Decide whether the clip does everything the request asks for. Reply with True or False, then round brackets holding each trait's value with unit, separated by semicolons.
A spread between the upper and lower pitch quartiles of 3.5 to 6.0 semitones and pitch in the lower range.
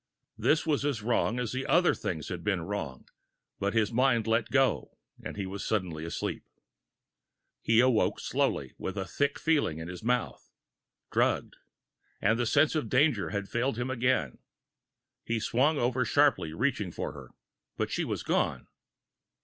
True (4.7 semitones; 115 Hz)